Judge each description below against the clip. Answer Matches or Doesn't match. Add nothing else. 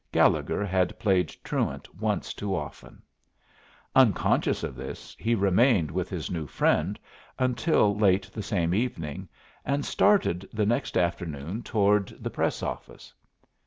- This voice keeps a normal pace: Doesn't match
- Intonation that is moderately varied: Matches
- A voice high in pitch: Doesn't match